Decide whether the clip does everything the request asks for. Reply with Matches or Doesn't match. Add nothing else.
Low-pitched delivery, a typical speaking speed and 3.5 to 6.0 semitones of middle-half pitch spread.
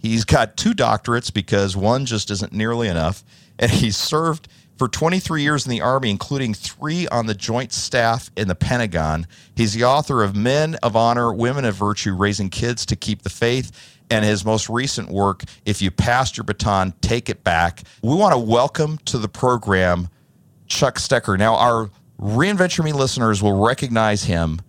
Matches